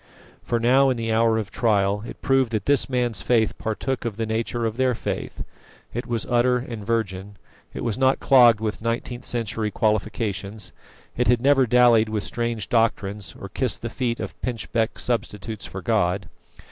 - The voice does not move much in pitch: Yes, narrow, 2.3 semitones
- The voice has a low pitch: Yes, low, 115 Hz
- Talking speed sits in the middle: Yes, average, 175 wpm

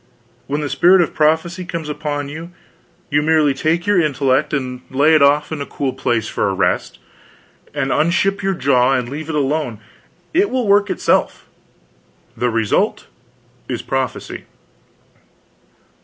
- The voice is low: No, medium, 150 Hz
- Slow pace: No, average, 150 wpm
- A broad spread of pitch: No, average, 3.6 semitones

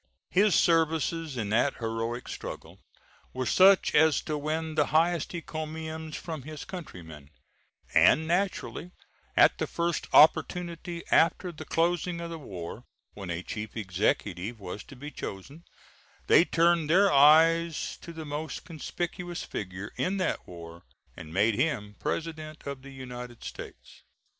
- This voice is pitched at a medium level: Yes, medium, 155 Hz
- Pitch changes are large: Yes, wide, 6.4 semitones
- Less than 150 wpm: Yes, average, 140 wpm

